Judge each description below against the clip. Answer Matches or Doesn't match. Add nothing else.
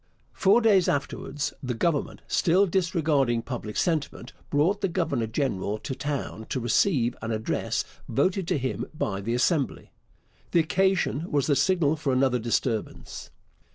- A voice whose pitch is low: Doesn't match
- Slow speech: Doesn't match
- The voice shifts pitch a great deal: Matches